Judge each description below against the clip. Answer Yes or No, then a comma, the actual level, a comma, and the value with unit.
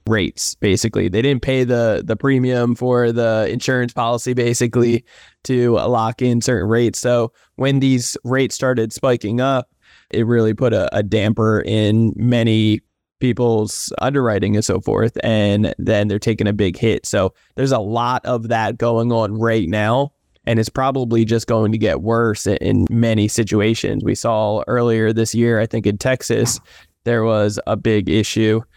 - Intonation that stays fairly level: Yes, narrow, 2.1 semitones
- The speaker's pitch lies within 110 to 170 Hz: Yes, low, 115 Hz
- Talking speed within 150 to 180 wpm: Yes, average, 165 wpm